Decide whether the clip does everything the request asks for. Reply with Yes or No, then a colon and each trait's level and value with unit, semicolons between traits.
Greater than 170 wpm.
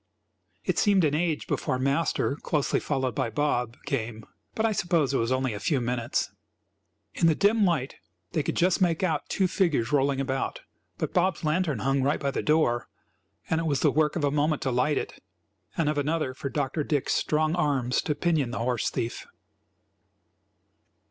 Yes: average, 185 wpm